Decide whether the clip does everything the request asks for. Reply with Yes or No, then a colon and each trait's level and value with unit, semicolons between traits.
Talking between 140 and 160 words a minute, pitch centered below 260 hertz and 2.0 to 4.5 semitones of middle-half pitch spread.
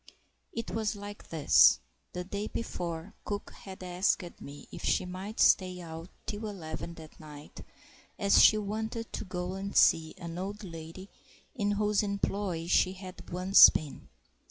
Yes: average, 155 wpm; medium, 185 Hz; average, 3.4 semitones